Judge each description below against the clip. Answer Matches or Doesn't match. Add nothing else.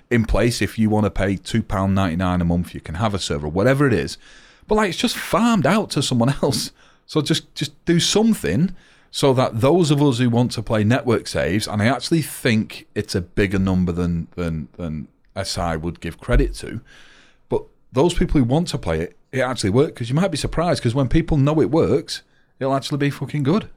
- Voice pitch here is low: Matches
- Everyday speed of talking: Doesn't match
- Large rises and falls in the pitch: Matches